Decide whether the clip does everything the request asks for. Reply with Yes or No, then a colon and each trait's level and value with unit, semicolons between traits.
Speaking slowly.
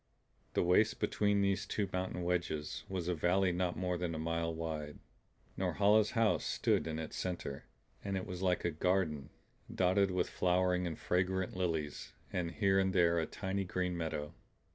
No: average, 170 wpm